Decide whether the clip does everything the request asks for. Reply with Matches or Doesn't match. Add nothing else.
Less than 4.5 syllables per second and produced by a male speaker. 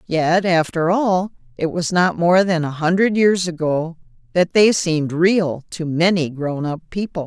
Doesn't match